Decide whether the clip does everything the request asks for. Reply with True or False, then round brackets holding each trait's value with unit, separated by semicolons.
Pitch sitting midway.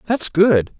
True (175 Hz)